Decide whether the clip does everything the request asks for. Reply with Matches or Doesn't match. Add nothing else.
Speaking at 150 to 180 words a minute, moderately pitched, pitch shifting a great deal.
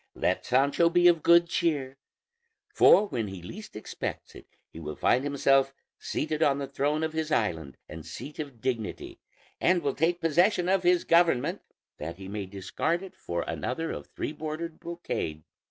Matches